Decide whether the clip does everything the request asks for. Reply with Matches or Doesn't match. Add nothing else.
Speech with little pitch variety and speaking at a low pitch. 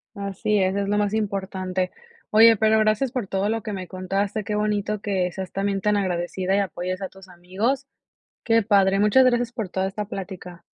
Doesn't match